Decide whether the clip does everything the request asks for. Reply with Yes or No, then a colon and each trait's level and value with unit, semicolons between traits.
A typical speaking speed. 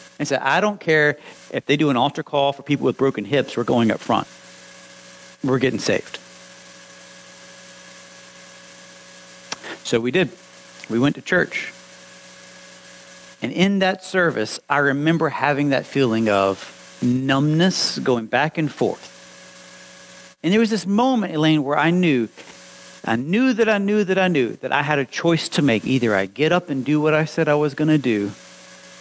Yes: average, 170 wpm